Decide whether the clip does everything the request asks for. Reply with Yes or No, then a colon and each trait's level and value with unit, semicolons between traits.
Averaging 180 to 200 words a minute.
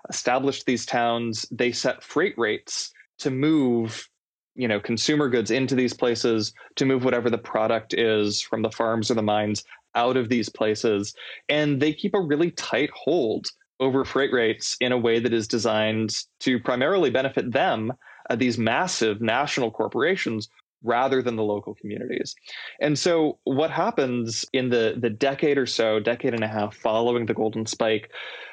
No: average, 170 wpm